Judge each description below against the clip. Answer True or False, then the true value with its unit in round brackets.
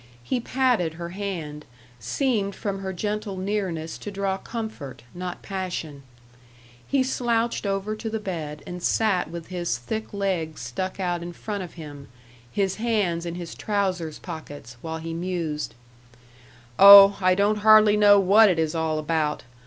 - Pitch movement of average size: True (4.1 semitones)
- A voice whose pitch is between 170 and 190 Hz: True (185 Hz)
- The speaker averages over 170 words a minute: False (155 wpm)